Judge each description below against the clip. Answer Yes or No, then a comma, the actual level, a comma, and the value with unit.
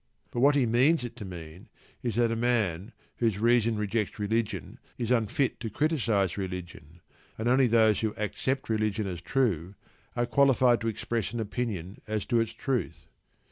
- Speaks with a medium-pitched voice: No, low, 115 Hz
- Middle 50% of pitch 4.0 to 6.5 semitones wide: No, average, 3.3 semitones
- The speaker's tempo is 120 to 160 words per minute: No, average, 175 wpm